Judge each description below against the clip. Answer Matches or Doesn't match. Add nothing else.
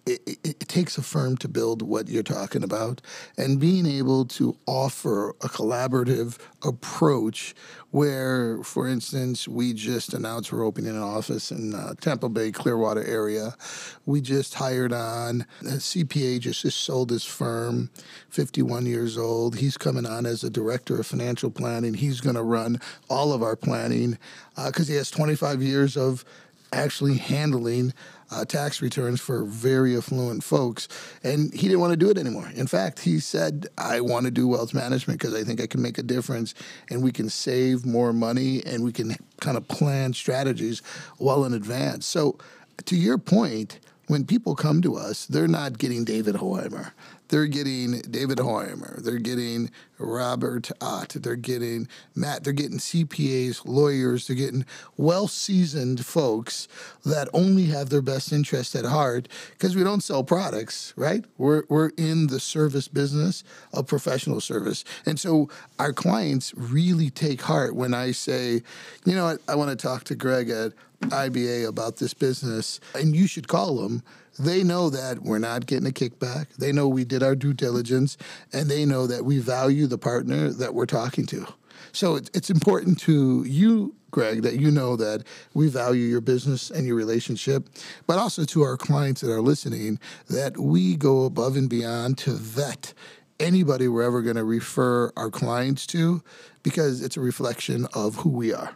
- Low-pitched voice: Matches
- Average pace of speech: Matches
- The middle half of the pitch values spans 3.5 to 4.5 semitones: Matches